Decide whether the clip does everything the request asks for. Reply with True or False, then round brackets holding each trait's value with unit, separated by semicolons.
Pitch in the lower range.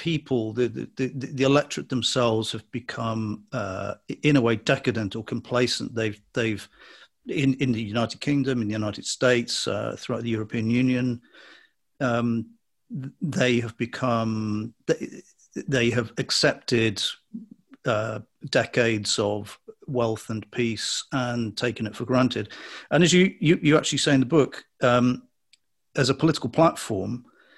True (120 Hz)